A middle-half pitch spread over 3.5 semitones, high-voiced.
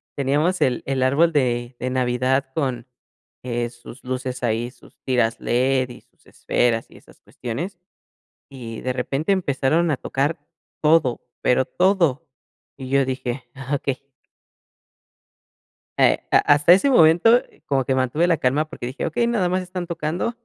No: average, 4.5 semitones; low, 135 Hz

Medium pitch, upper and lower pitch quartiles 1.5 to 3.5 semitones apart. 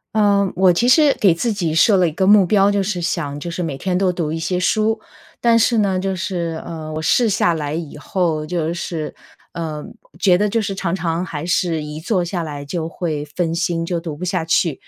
Yes: medium, 175 Hz; average, 3.2 semitones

